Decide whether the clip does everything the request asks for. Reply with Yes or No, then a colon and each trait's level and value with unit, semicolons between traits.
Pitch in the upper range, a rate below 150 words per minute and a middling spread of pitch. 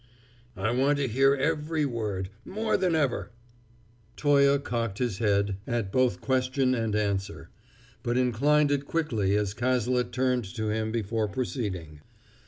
No: low, 120 Hz; average, 140 wpm; average, 4.6 semitones